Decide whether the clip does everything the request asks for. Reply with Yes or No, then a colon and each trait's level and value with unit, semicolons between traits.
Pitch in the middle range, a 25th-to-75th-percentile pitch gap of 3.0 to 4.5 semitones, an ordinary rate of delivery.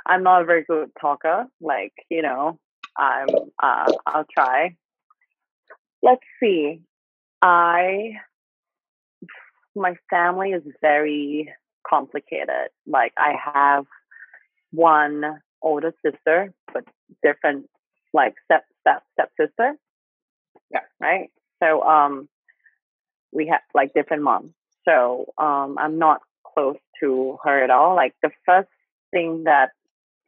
No: medium, 160 Hz; average, 3.8 semitones; slow, 115 wpm